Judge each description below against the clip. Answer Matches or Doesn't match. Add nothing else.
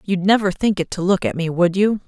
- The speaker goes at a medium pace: Doesn't match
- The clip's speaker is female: Matches